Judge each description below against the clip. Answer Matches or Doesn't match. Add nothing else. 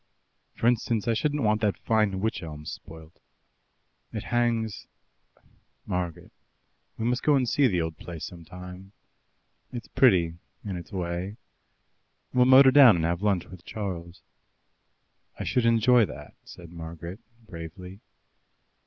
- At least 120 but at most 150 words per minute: Matches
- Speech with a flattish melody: Doesn't match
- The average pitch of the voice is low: Matches